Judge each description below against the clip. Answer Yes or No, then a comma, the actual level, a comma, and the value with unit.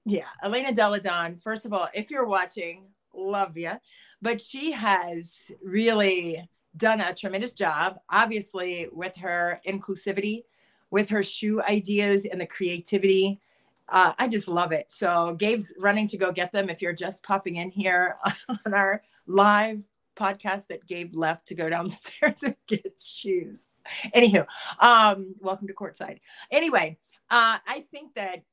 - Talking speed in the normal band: Yes, average, 150 wpm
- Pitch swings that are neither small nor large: Yes, average, 3.0 semitones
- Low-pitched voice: No, high, 195 Hz